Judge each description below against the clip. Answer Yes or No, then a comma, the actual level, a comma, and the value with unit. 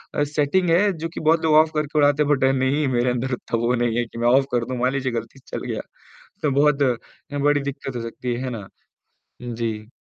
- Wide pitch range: No, average, 3.5 semitones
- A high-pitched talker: No, low, 135 Hz